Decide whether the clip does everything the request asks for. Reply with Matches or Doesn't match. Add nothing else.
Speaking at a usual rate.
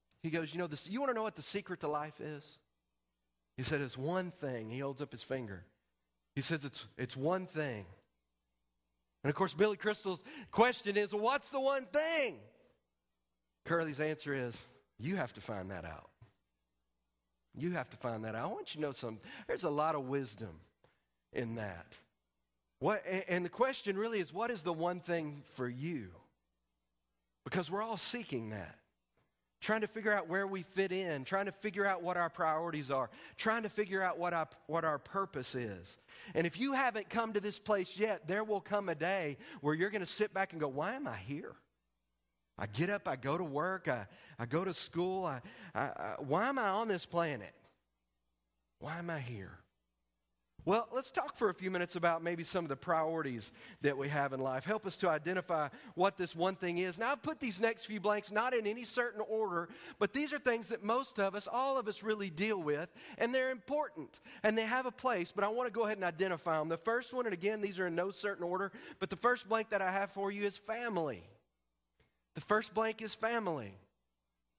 Doesn't match